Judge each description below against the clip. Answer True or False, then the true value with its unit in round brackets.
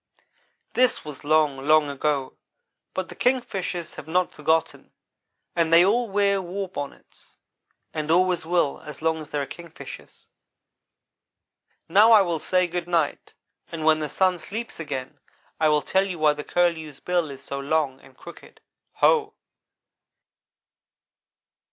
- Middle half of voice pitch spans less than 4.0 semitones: True (3.4 semitones)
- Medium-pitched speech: True (165 Hz)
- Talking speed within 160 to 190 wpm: False (145 wpm)